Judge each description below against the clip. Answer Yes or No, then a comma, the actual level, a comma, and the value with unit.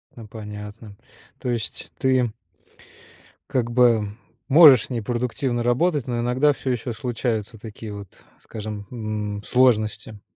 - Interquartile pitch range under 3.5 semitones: Yes, average, 2.8 semitones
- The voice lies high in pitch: No, low, 120 Hz